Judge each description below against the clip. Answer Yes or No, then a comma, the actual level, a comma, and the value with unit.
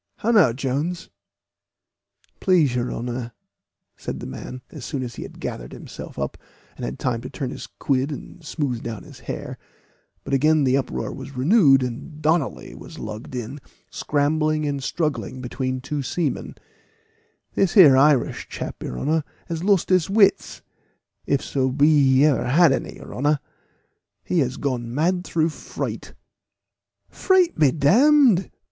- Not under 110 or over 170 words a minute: Yes, average, 155 wpm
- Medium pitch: Yes, medium, 145 Hz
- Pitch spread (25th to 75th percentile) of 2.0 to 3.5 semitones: No, average, 4.0 semitones